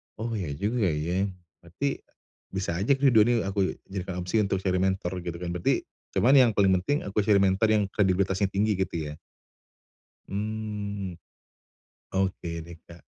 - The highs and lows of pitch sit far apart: No, average, 2.8 semitones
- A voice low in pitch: Yes, very low, 95 Hz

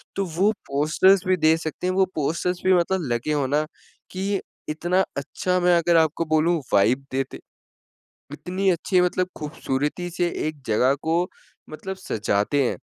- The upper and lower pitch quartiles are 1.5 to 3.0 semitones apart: No, average, 3.8 semitones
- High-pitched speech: No, medium, 165 Hz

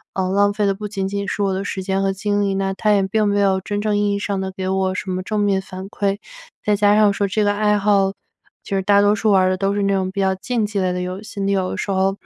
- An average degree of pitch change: No, narrow, 1.2 semitones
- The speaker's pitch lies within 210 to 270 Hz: No, high, 200 Hz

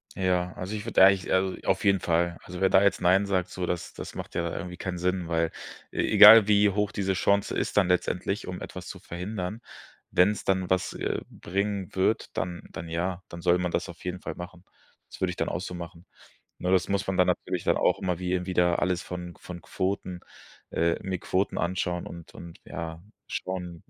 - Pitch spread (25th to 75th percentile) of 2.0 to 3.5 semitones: No, narrow, 1.5 semitones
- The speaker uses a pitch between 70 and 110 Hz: Yes, very low, 90 Hz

